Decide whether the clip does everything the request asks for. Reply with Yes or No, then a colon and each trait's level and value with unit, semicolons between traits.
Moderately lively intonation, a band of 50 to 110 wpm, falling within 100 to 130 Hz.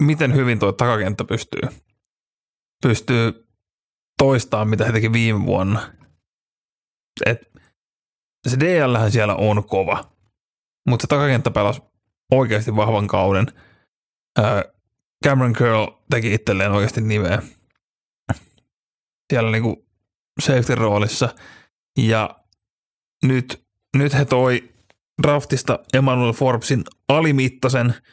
Yes: average, 3.6 semitones; slow, 95 wpm; low, 115 Hz